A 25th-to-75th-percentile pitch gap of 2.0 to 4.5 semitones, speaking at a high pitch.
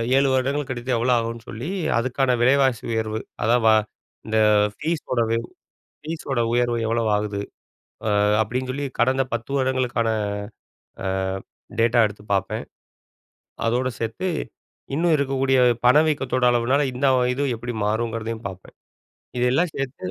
No: average, 2.7 semitones; low, 125 Hz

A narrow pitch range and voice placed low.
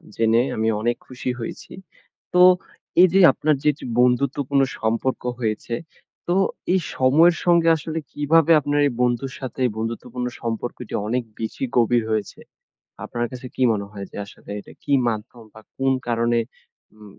No: average, 3.9 semitones; low, 125 Hz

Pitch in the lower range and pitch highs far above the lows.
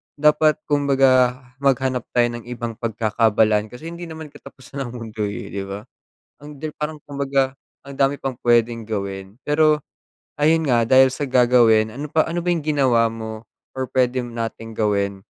No: low, 125 Hz; average, 4.1 semitones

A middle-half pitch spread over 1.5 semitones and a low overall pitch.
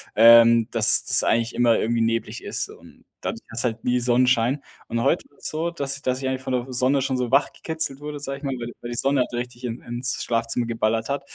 Yes: narrow, 2.6 semitones; low, 125 Hz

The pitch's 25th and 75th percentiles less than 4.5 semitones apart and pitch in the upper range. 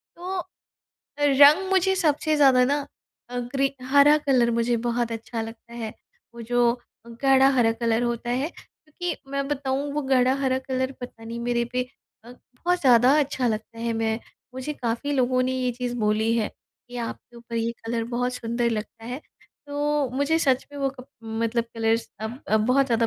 Yes: average, 3.1 semitones; very high, 250 Hz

